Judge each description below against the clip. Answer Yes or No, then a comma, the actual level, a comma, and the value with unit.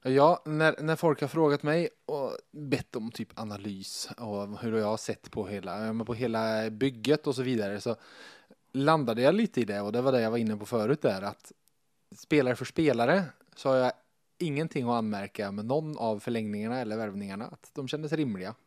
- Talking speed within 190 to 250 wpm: Yes, fast, 195 wpm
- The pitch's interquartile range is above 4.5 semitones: Yes, wide, 5.5 semitones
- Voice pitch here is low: Yes, low, 125 Hz